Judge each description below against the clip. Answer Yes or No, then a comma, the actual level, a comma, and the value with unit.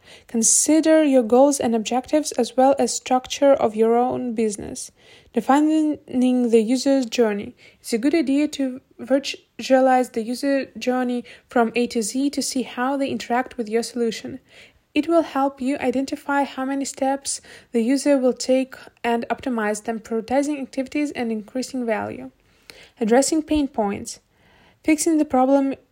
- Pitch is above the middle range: Yes, very high, 255 Hz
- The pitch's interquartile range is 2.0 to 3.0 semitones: Yes, narrow, 2.6 semitones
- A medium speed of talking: Yes, average, 150 wpm